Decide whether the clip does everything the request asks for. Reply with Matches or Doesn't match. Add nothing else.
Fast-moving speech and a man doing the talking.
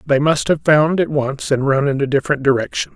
Matches